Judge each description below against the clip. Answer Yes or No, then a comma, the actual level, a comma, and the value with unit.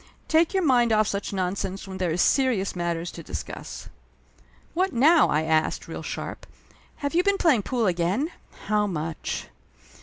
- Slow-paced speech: No, average, 160 wpm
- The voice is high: Yes, high, 205 Hz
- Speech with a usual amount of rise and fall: No, wide, 8.4 semitones